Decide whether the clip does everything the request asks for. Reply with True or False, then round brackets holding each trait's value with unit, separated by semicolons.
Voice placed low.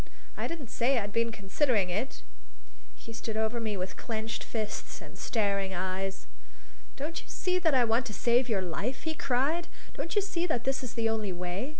False (230 Hz)